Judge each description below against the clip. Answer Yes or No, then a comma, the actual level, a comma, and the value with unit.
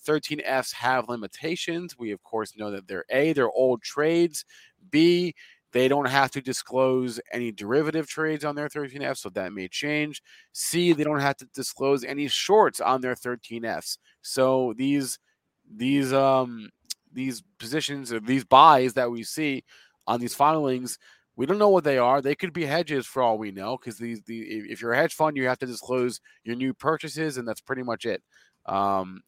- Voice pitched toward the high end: No, low, 130 Hz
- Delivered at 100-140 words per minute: No, average, 185 wpm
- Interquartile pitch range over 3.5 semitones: Yes, average, 3.9 semitones